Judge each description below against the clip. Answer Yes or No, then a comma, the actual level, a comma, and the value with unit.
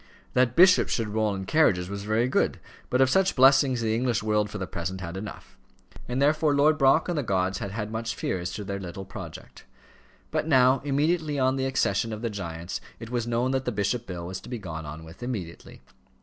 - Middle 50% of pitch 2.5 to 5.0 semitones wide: No, wide, 5.5 semitones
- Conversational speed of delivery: No, fast, 220 wpm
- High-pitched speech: No, low, 115 Hz